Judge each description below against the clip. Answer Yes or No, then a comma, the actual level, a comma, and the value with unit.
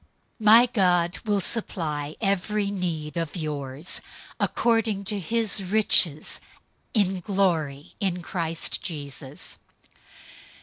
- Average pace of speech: No, slow, 100 wpm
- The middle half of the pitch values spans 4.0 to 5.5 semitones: Yes, average, 4.8 semitones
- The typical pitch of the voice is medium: Yes, medium, 180 Hz